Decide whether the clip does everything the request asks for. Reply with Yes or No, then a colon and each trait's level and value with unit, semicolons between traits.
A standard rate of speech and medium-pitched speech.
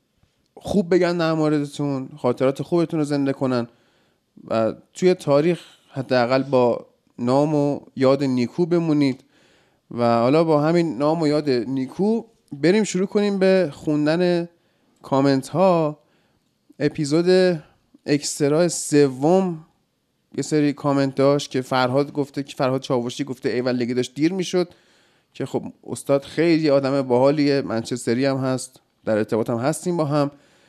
Yes: average, 135 wpm; medium, 145 Hz